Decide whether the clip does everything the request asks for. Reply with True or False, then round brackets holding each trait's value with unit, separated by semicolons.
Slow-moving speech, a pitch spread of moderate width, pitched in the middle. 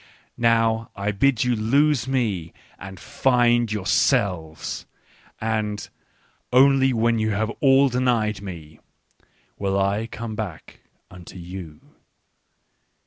False (95 wpm; 4.0 semitones; 110 Hz)